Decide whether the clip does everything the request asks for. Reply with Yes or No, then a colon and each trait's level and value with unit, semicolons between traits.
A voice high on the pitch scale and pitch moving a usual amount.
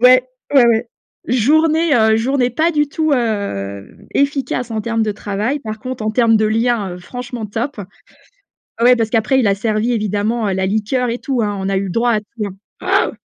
Yes: high, 230 Hz; average, 3.0 semitones